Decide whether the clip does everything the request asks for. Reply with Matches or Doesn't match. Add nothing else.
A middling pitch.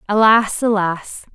Doesn't match